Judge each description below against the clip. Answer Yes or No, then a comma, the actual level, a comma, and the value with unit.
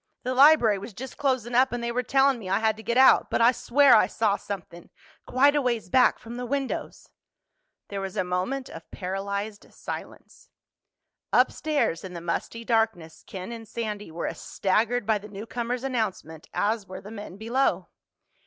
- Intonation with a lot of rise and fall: No, average, 4.1 semitones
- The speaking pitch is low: No, high, 225 Hz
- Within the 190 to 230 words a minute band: No, average, 180 wpm